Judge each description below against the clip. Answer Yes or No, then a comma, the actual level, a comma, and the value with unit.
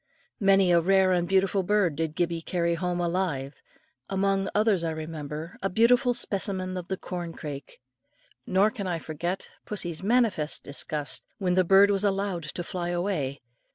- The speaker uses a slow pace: No, average, 160 wpm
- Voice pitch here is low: No, medium, 180 Hz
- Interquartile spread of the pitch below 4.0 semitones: Yes, average, 2.8 semitones